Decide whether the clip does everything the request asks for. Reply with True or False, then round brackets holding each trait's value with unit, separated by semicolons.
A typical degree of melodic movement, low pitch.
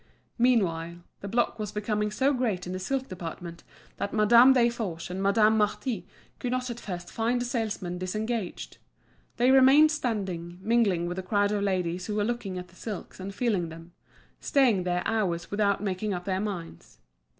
False (4.6 semitones; 205 Hz)